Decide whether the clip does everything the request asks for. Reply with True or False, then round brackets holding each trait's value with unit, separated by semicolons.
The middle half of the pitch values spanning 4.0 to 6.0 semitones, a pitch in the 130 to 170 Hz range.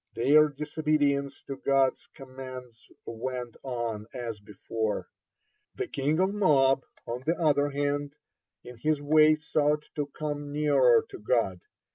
False (3.4 semitones; 140 Hz)